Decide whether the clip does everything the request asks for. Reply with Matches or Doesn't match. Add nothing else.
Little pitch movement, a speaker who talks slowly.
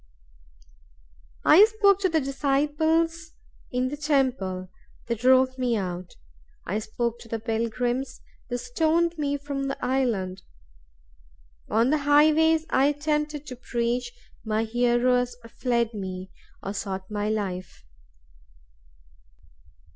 Doesn't match